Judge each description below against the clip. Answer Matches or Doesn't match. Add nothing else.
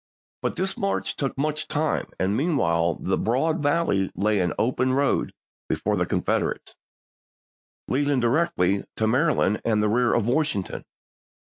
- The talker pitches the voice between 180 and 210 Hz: Doesn't match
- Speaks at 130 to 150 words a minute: Matches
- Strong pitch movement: Matches